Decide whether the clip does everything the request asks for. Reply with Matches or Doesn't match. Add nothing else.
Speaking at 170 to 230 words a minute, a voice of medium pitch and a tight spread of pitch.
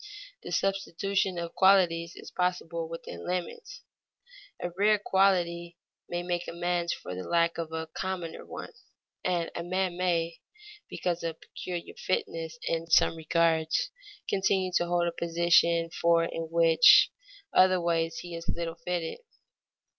Doesn't match